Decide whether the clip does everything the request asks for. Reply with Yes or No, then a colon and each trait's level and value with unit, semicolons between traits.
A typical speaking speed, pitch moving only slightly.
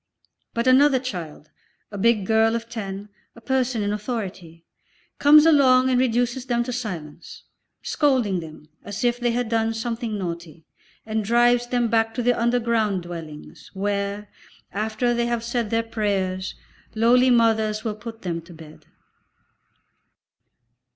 No: average, 145 wpm; average, 3.4 semitones